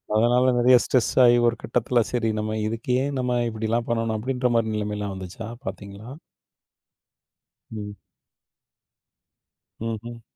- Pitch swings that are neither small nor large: No, narrow, 2.1 semitones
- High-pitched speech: No, low, 115 Hz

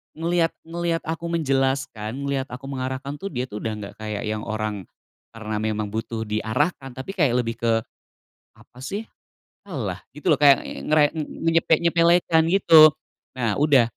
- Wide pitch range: Yes, wide, 6.6 semitones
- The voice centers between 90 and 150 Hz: Yes, low, 135 Hz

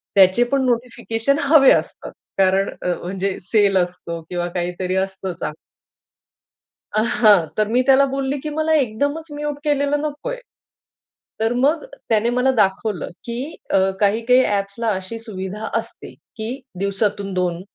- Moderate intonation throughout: No, wide, 5.8 semitones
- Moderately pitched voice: No, high, 220 Hz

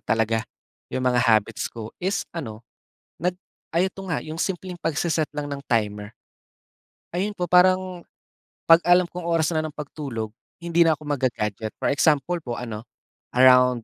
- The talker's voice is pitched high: No, medium, 150 Hz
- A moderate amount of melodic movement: No, wide, 6.6 semitones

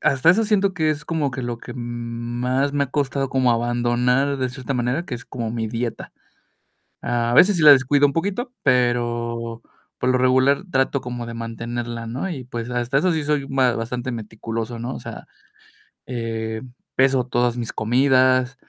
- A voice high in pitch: No, low, 125 Hz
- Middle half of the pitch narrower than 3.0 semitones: Yes, narrow, 2.6 semitones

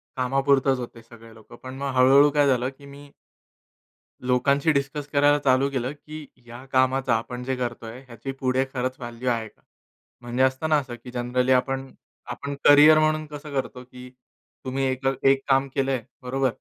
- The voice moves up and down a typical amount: No, narrow, 1.9 semitones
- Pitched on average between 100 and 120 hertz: No, low, 130 Hz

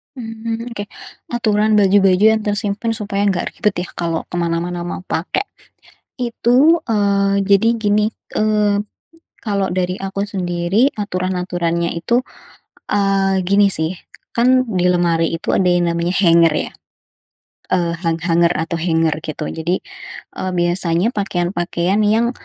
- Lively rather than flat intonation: No, average, 3.4 semitones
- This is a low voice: No, high, 190 Hz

